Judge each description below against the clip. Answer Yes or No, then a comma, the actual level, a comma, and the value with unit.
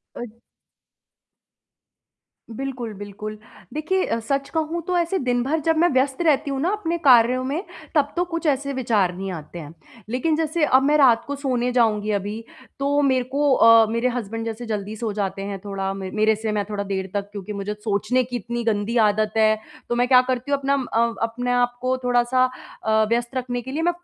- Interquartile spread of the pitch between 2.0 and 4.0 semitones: No, average, 4.4 semitones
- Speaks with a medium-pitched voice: No, high, 245 Hz